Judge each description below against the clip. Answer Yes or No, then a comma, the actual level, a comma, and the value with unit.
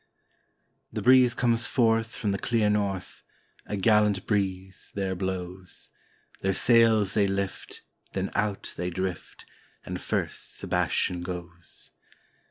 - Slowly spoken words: Yes, slow, 125 wpm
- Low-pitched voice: Yes, low, 100 Hz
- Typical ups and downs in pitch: Yes, average, 3.0 semitones